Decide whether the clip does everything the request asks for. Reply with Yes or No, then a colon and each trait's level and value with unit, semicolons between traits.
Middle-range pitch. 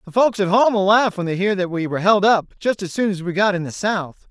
No: high, 195 Hz